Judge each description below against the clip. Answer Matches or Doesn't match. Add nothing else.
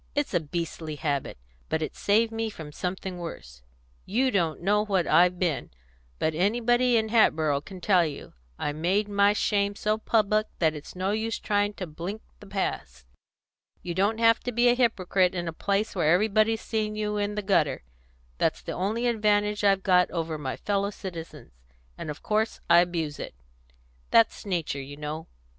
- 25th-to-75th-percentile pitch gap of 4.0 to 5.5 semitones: Matches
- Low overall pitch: Doesn't match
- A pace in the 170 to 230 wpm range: Matches